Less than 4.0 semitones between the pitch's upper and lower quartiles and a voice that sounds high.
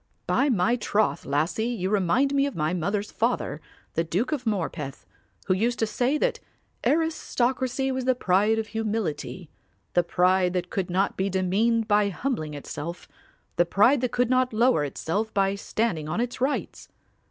No: wide, 5.5 semitones; high, 210 Hz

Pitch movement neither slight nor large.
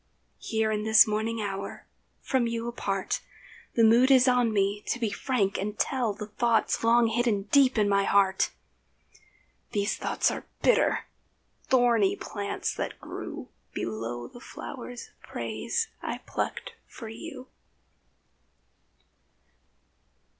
Yes: average, 3.2 semitones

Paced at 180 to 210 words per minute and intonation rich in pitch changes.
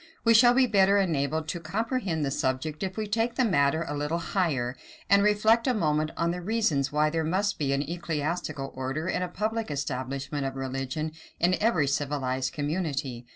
Yes: average, 185 wpm; wide, 6.1 semitones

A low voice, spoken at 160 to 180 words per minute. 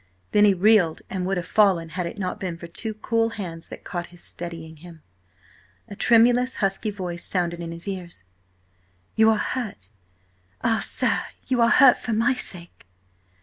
No: high, 190 Hz; average, 175 wpm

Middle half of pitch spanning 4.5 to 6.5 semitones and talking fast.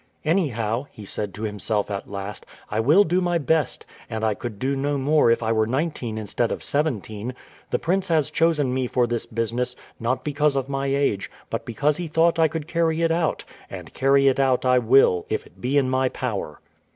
Yes: average, 5.1 semitones; fast, 210 wpm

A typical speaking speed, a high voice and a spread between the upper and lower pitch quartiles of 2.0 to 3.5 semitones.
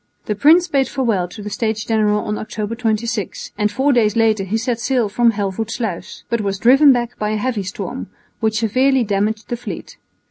Yes: average, 190 wpm; high, 220 Hz; narrow, 2.6 semitones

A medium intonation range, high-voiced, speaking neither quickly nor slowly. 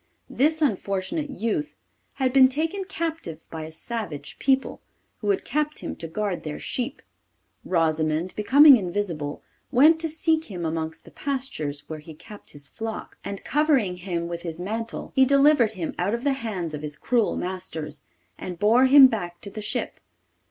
No: wide, 8.3 semitones; high, 210 Hz; average, 170 wpm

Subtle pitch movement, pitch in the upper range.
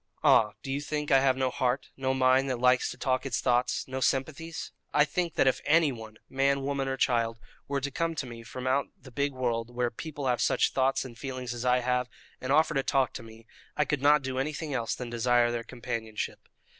No: narrow, 2.3 semitones; low, 130 Hz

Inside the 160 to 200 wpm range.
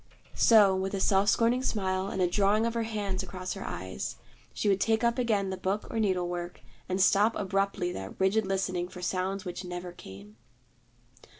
Yes: average, 190 wpm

